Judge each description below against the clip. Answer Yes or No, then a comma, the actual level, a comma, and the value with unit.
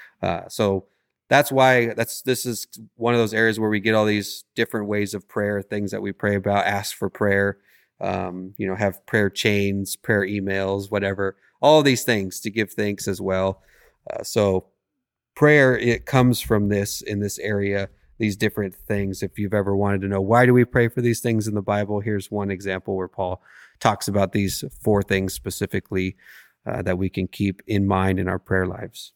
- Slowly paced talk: No, average, 200 wpm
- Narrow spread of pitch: Yes, narrow, 2.0 semitones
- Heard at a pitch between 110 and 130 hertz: No, low, 100 Hz